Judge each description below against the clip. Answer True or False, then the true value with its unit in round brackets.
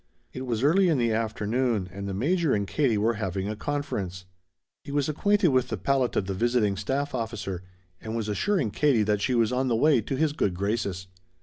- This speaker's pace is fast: True (210 wpm)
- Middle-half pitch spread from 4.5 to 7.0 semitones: True (5.4 semitones)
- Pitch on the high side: False (115 Hz)